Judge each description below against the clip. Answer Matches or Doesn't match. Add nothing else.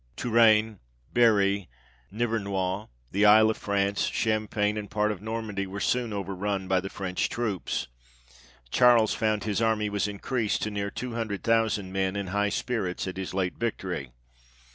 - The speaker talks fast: Doesn't match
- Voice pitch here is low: Matches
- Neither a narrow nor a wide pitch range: Doesn't match